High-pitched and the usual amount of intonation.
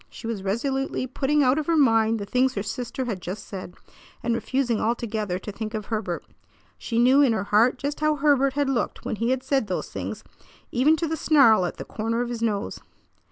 Yes: high, 235 Hz; average, 4.0 semitones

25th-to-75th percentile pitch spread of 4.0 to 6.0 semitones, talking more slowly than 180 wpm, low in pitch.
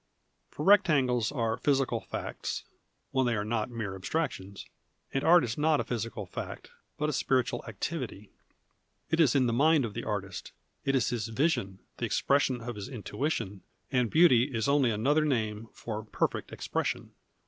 Yes: average, 4.7 semitones; average, 170 wpm; low, 120 Hz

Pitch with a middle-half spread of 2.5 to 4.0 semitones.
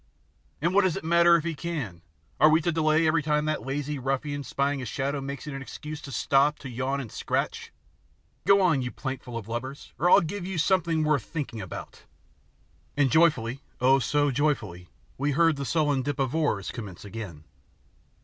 Yes: average, 3.3 semitones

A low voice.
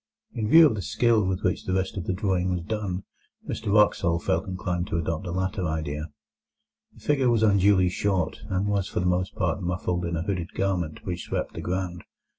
Yes: very low, 95 Hz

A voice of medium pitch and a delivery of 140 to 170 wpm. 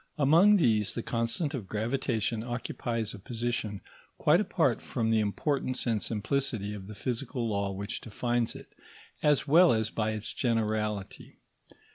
No: low, 115 Hz; average, 145 wpm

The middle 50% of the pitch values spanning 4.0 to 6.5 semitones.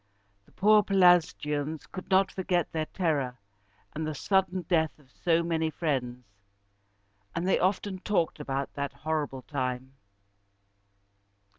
Yes: average, 4.3 semitones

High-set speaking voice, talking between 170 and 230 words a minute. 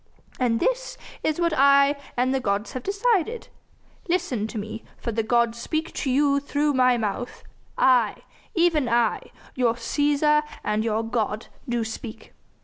No: very high, 255 Hz; average, 150 wpm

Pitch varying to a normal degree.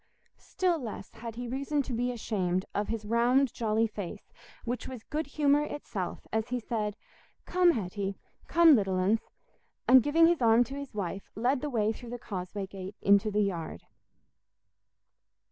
Yes: average, 4.5 semitones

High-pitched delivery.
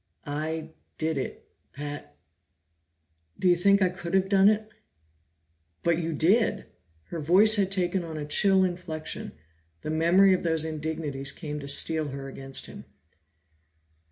No: medium, 165 Hz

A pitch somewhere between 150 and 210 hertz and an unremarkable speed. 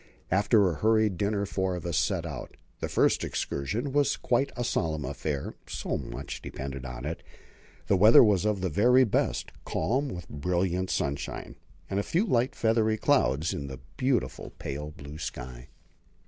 No: very low, 95 Hz; average, 165 wpm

